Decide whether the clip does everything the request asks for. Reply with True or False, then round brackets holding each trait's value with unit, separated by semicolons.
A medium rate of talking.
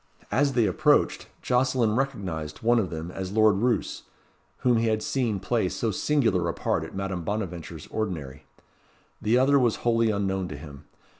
True (165 wpm)